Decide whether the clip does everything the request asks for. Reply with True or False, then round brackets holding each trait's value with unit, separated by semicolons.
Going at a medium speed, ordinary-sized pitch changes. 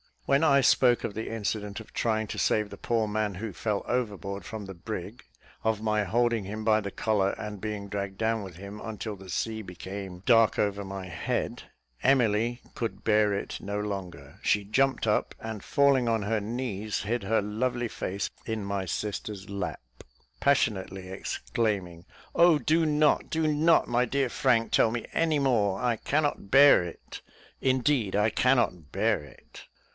True (170 wpm; 3.4 semitones)